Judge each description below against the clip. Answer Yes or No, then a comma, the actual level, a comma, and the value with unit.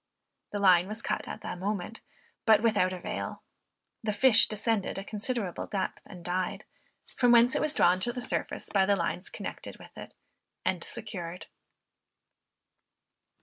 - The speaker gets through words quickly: No, average, 150 wpm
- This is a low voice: No, high, 205 Hz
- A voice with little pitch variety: No, average, 3.6 semitones